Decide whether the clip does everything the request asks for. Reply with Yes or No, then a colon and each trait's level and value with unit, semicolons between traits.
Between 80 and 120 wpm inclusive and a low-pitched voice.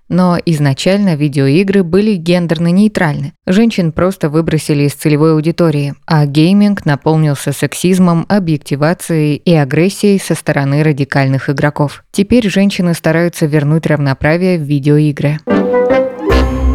No: slow, 110 wpm; medium, 160 Hz